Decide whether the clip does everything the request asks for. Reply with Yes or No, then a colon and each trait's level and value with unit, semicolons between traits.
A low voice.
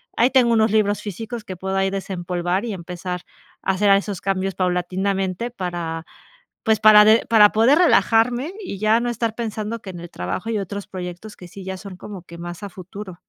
No: high, 195 Hz